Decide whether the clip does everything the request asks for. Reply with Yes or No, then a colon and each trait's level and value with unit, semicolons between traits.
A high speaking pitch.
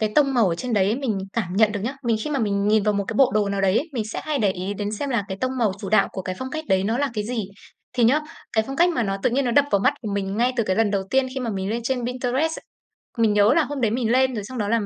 Yes: high, 225 Hz